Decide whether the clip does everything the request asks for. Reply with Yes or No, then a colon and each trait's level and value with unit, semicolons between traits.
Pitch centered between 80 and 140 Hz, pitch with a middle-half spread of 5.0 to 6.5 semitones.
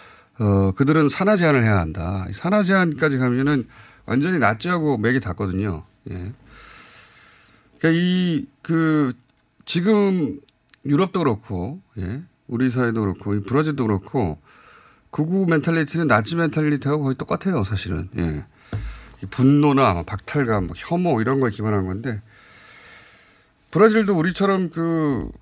No: low, 135 Hz; wide, 7.9 semitones